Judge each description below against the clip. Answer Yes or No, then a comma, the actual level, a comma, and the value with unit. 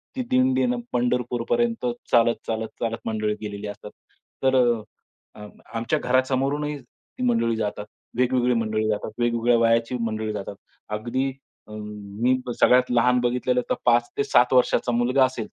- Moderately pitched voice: No, low, 120 Hz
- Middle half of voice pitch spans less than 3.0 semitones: Yes, narrow, 2.5 semitones